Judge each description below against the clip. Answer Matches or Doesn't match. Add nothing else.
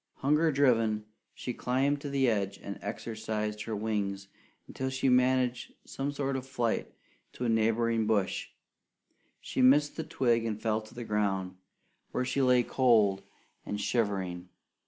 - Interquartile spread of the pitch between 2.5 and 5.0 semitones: Matches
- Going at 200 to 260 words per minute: Doesn't match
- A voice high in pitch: Doesn't match